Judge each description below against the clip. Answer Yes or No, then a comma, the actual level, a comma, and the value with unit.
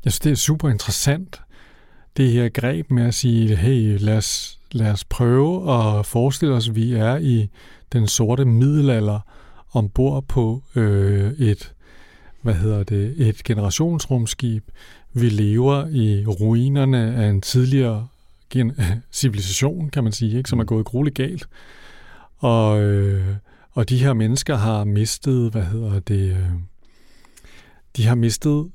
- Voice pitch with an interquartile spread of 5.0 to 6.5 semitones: No, average, 3.8 semitones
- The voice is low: Yes, low, 115 Hz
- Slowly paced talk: Yes, slow, 140 wpm